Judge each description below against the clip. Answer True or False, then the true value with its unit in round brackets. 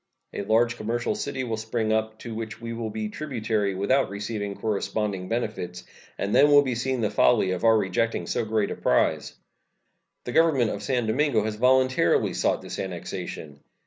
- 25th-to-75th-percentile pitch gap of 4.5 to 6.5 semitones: False (2.9 semitones)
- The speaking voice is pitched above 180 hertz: False (110 Hz)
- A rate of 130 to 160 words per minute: False (175 wpm)